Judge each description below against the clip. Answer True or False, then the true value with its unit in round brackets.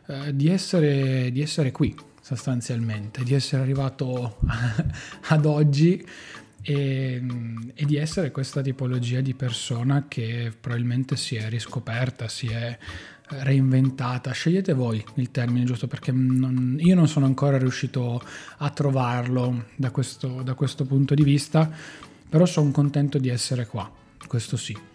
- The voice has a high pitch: False (130 Hz)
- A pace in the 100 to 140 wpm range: True (135 wpm)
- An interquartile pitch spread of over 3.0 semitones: False (2.7 semitones)